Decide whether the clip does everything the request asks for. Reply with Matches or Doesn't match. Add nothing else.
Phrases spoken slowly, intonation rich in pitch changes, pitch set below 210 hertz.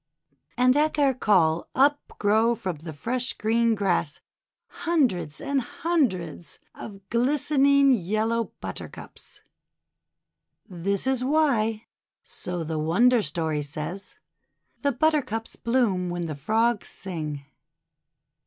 Doesn't match